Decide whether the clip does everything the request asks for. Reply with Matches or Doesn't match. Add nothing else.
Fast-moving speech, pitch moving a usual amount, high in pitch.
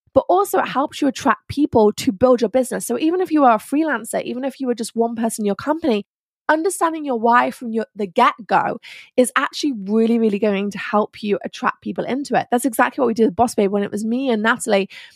Matches